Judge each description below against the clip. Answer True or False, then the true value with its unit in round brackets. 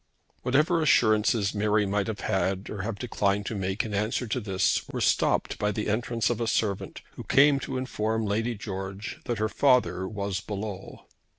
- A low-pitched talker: True (105 Hz)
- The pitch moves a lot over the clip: False (2.8 semitones)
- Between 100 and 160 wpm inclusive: False (180 wpm)